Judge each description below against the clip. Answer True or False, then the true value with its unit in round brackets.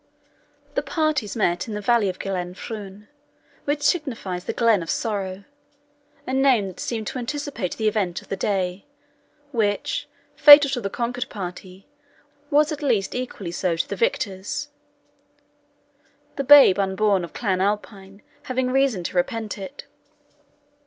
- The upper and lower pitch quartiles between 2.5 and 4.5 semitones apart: False (5.2 semitones)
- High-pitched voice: True (210 Hz)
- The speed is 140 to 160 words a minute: True (145 wpm)